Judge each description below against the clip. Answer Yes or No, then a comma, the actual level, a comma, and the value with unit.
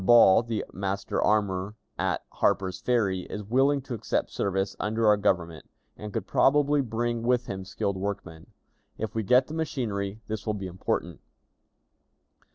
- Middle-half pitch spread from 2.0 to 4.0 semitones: Yes, average, 3.5 semitones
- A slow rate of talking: No, average, 155 wpm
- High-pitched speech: No, low, 105 Hz